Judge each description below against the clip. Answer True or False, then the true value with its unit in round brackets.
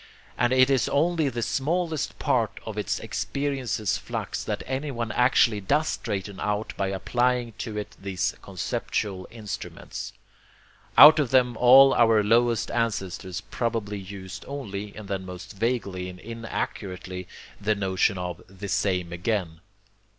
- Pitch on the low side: True (105 Hz)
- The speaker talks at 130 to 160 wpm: True (135 wpm)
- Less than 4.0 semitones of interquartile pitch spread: False (4.3 semitones)